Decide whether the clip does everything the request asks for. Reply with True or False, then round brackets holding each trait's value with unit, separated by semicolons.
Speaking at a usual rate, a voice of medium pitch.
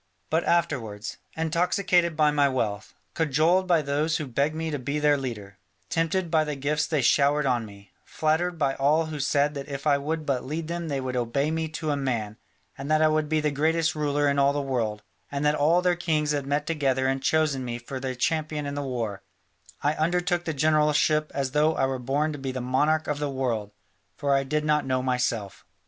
False (220 wpm; 145 Hz)